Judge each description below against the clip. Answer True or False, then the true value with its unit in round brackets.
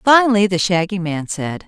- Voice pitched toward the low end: False (190 Hz)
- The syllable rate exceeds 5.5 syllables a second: False (5.1 syllables/s)